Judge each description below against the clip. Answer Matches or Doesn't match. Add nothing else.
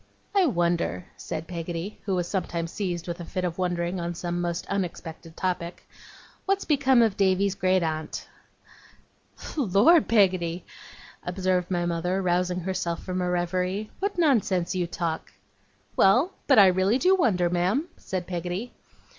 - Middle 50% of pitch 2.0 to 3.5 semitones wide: Matches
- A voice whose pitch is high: Doesn't match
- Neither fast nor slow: Matches